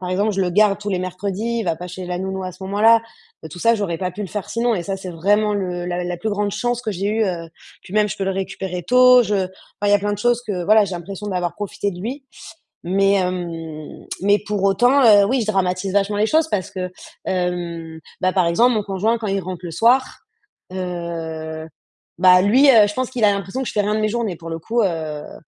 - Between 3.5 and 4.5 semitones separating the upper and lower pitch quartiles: No, average, 3.0 semitones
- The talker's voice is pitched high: Yes, high, 195 Hz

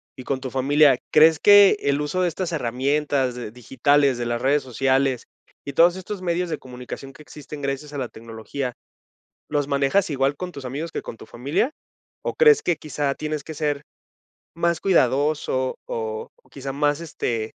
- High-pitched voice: No, medium, 140 Hz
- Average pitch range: Yes, average, 3.0 semitones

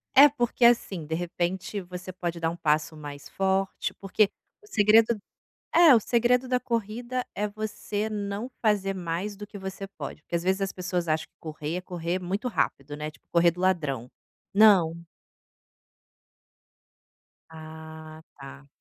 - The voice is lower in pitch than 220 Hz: Yes, medium, 185 Hz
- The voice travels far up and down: No, average, 4.6 semitones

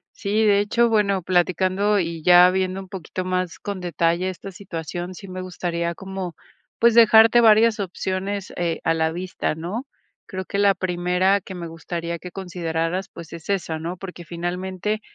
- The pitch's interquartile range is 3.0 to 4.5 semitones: No, narrow, 2.5 semitones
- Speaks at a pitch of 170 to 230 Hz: Yes, medium, 185 Hz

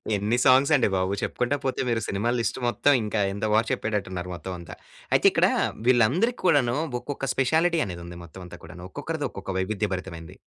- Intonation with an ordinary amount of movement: No, wide, 5.9 semitones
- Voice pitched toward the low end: Yes, low, 110 Hz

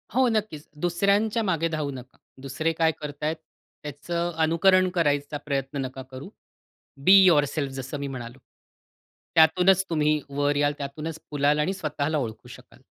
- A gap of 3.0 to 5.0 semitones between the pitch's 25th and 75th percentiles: Yes, average, 3.3 semitones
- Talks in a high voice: No, medium, 150 Hz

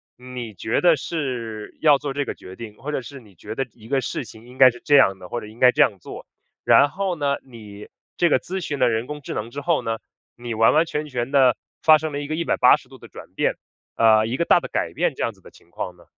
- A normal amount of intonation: Yes, average, 4.4 semitones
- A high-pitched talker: No, low, 125 Hz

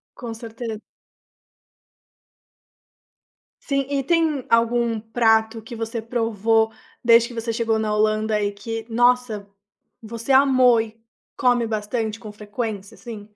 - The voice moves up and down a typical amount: No, narrow, 1.8 semitones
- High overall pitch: Yes, high, 225 Hz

